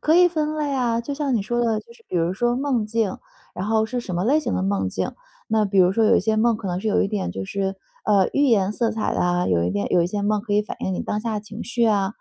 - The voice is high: Yes, high, 215 Hz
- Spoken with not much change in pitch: No, average, 3.8 semitones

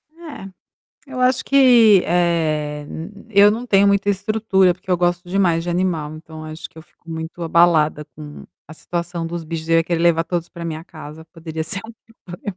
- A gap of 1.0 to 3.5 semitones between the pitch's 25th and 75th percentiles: Yes, average, 3.2 semitones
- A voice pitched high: No, medium, 170 Hz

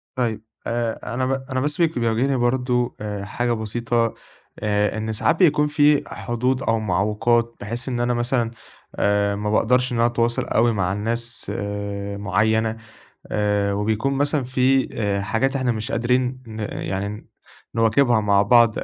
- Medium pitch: No, low, 115 Hz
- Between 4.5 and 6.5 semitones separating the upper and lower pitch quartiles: No, average, 3.1 semitones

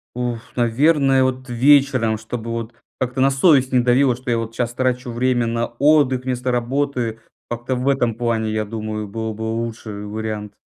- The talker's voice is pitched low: Yes, low, 120 Hz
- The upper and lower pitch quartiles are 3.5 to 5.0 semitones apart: No, narrow, 2.4 semitones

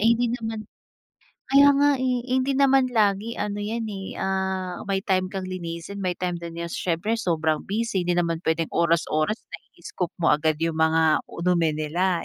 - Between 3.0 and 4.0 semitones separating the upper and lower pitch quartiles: No, average, 4.7 semitones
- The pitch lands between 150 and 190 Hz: Yes, medium, 185 Hz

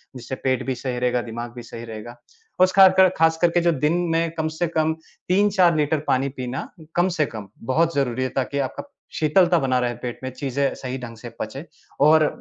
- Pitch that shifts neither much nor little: Yes, average, 4.8 semitones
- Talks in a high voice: No, medium, 140 Hz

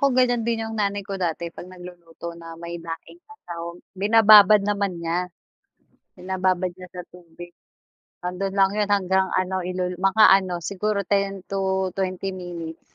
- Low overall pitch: No, medium, 185 Hz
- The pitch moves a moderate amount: No, narrow, 2.3 semitones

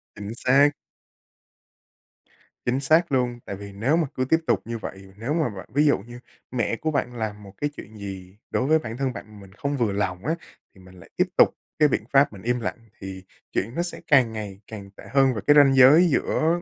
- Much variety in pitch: Yes, wide, 5.8 semitones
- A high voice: No, low, 120 Hz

